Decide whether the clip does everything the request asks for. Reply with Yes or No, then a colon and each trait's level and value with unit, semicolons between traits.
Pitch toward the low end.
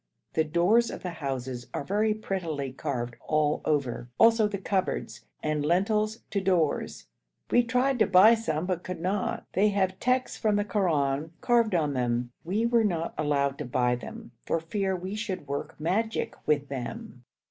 No: medium, 180 Hz